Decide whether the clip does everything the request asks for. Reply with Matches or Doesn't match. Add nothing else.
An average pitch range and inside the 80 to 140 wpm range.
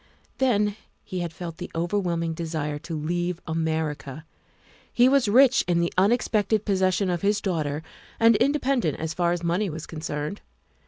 Doesn't match